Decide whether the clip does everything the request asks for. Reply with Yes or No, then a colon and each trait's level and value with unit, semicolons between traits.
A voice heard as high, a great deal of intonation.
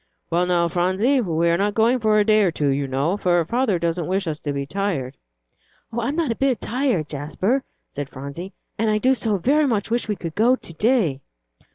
Yes: high, 195 Hz; wide, 5.9 semitones